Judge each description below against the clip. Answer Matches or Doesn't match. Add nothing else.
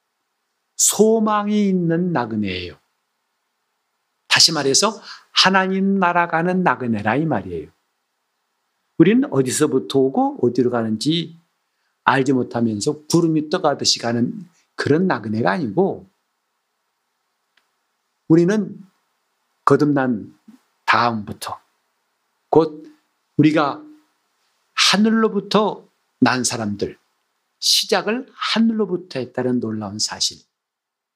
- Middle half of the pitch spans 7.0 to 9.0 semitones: Matches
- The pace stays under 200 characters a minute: Doesn't match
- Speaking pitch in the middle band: Matches